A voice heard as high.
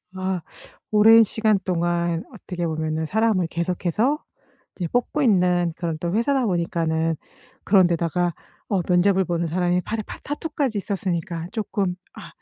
No: medium, 180 Hz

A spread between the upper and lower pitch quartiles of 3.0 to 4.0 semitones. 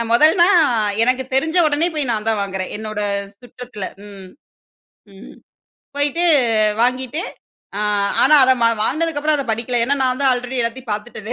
No: average, 4.7 semitones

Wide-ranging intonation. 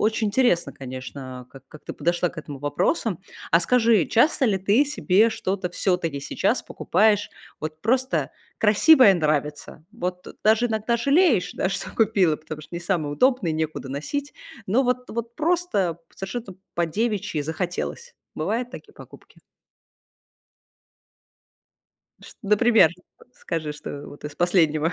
Yes: wide, 6.9 semitones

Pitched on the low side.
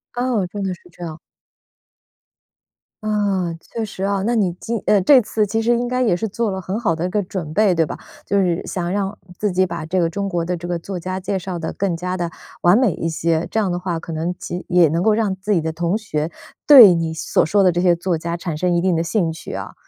No: medium, 185 Hz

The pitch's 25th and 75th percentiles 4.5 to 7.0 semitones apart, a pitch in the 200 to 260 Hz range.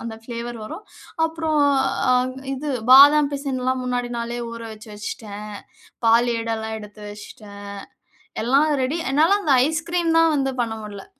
Yes: average, 5.0 semitones; very high, 250 Hz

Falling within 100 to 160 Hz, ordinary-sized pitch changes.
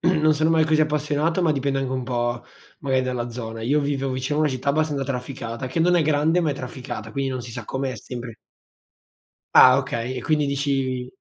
Yes: low, 135 Hz; average, 3.1 semitones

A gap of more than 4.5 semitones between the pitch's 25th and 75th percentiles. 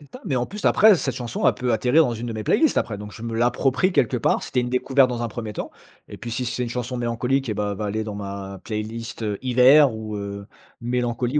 No: average, 2.8 semitones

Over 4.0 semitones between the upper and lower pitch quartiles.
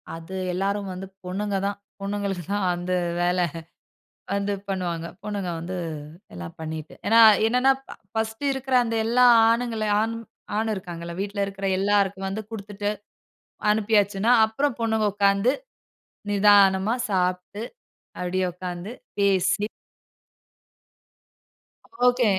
No: average, 2.9 semitones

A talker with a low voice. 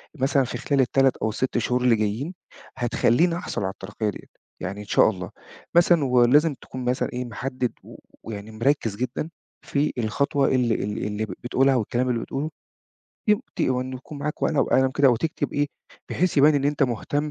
Yes: low, 130 Hz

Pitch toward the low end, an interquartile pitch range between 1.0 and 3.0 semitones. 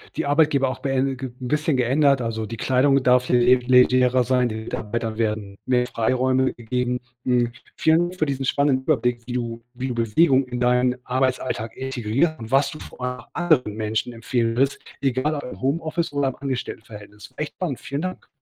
Yes: low, 125 Hz; narrow, 2.5 semitones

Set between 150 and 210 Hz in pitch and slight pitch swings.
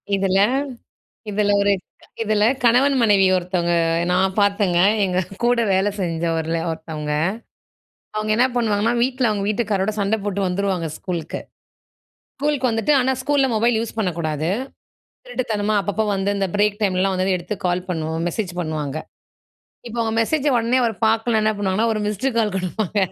No: high, 205 Hz; average, 3.6 semitones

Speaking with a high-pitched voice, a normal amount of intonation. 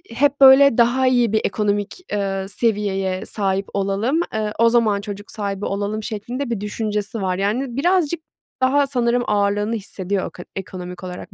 Yes: high, 210 Hz; average, 3.5 semitones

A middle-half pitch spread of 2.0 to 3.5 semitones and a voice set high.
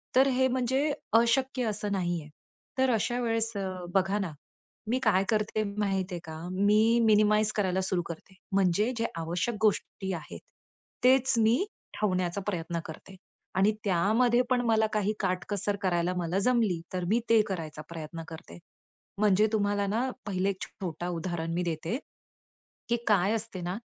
No: average, 3.9 semitones; high, 200 Hz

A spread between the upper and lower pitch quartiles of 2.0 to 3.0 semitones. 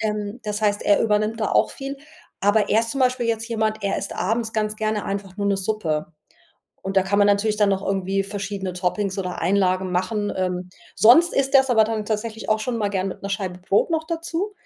Yes: narrow, 2.4 semitones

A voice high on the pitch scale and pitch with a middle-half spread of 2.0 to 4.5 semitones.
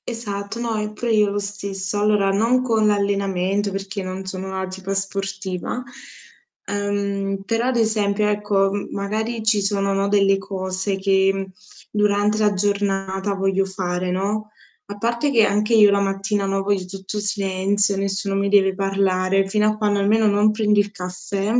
No: high, 200 Hz; narrow, 1.3 semitones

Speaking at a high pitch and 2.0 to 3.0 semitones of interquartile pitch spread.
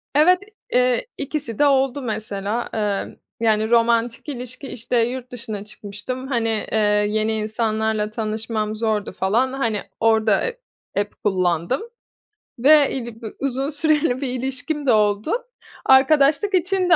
No: high, 235 Hz; average, 4.0 semitones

